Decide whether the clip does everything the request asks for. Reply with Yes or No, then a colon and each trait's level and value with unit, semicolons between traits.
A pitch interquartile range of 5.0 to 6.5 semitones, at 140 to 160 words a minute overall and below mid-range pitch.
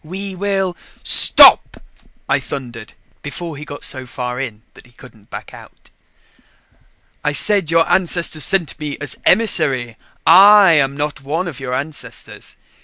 No: average, 5.3 semitones; average, 150 wpm; medium, 150 Hz